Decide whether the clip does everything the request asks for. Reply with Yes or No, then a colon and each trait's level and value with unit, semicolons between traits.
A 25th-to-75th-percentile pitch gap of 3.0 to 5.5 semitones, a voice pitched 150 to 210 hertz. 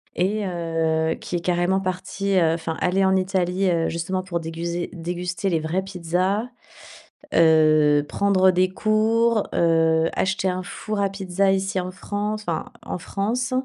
No: narrow, 2.6 semitones; medium, 185 Hz